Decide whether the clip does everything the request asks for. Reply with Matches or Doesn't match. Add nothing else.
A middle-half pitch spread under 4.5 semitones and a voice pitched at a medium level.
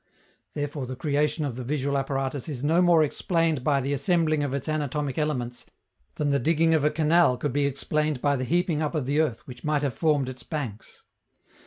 Matches